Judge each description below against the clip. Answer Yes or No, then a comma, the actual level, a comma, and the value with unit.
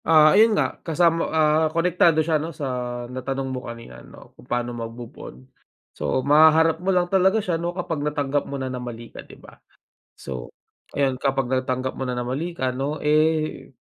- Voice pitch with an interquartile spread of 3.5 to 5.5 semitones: Yes, average, 4.2 semitones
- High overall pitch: No, medium, 145 Hz